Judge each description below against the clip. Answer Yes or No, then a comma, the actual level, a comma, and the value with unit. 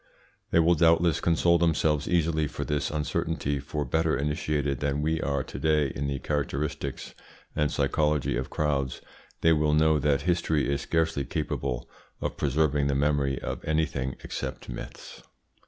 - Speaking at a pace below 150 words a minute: No, average, 155 wpm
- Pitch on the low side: Yes, very low, 75 Hz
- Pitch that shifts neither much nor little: No, narrow, 2.1 semitones